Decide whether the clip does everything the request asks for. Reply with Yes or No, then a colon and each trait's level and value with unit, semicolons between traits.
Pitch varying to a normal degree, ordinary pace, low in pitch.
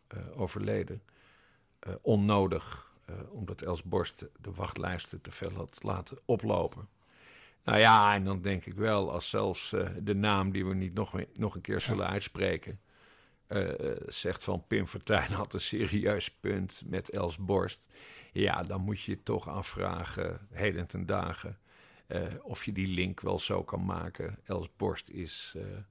No: narrow, 1.7 semitones; average, 165 wpm; low, 100 Hz